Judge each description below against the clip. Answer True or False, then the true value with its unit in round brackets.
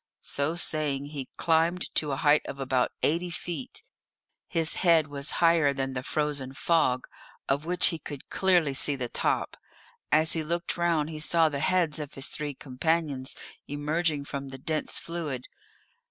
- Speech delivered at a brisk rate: False (165 wpm)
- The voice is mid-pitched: True (150 Hz)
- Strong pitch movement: False (3.1 semitones)